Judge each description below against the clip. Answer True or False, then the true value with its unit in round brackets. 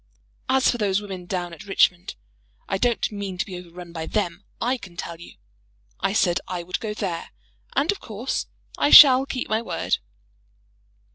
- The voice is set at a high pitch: True (195 Hz)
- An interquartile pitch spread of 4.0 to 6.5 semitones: True (4.5 semitones)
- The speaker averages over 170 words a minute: True (180 wpm)